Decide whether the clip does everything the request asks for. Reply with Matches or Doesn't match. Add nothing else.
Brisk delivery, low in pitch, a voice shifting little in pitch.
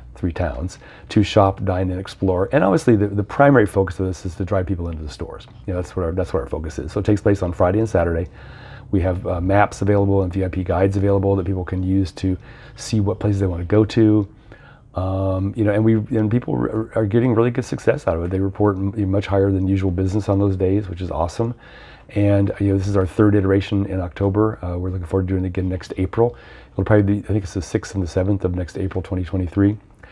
Matches